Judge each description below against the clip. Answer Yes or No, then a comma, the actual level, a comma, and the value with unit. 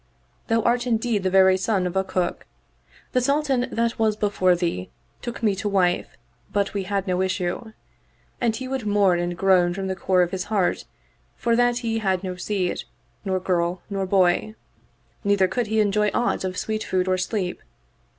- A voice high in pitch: Yes, high, 195 Hz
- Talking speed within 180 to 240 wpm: Yes, average, 185 wpm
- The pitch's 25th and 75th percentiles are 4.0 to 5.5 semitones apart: No, average, 3.2 semitones